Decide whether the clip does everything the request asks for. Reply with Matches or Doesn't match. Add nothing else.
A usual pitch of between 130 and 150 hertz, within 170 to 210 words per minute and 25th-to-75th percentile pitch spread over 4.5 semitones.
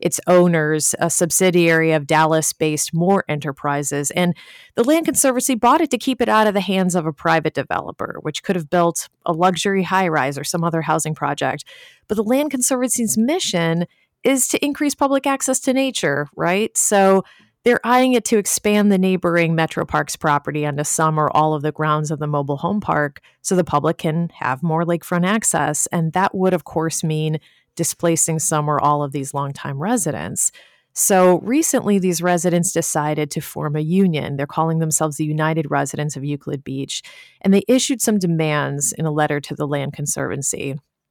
Doesn't match